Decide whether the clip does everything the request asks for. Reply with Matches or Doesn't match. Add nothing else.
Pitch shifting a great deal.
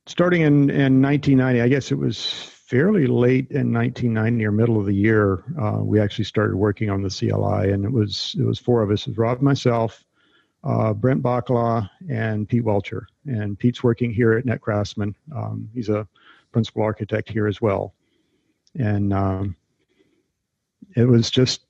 Doesn't match